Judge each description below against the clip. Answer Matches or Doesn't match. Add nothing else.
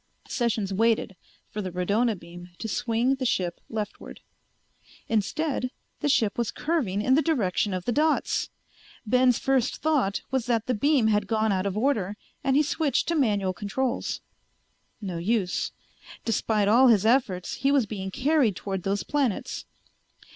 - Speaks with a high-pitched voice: Matches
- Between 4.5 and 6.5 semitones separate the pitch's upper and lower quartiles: Matches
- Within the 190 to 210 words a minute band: Doesn't match